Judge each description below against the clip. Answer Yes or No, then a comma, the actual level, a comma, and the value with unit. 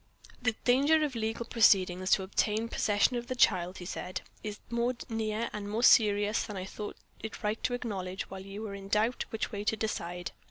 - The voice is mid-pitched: No, high, 210 Hz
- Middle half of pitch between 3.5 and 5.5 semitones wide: No, average, 2.9 semitones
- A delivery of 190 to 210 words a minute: Yes, average, 200 wpm